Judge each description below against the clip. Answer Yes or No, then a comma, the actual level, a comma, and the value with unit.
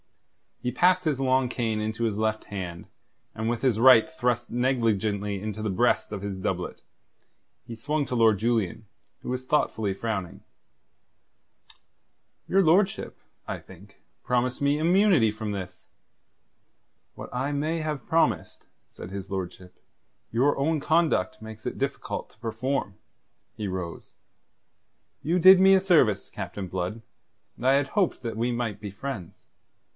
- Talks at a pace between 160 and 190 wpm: No, average, 145 wpm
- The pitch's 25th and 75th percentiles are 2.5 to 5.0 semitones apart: No, wide, 5.4 semitones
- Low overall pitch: Yes, low, 115 Hz